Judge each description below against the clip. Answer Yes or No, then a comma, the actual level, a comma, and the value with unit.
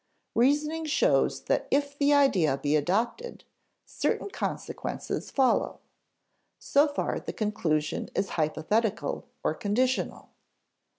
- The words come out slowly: Yes, slow, 105 wpm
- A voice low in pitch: No, high, 235 Hz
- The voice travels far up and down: Yes, wide, 8.2 semitones